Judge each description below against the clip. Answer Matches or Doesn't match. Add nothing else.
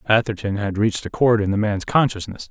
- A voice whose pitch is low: Matches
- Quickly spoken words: Matches